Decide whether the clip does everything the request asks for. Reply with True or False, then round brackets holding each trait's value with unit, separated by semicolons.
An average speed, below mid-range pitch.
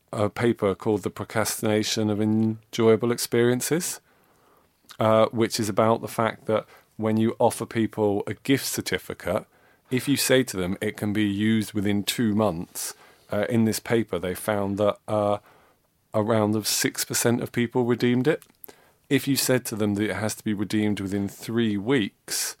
True (165 wpm; 110 Hz)